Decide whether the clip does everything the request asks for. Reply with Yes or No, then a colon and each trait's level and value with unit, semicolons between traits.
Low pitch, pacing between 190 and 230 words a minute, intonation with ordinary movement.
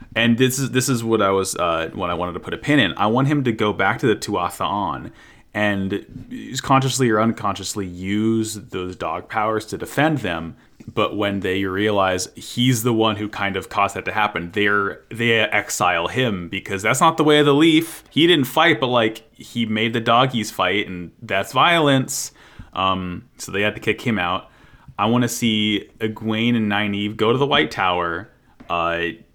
Yes: low, 110 Hz; average, 200 wpm; average, 3.7 semitones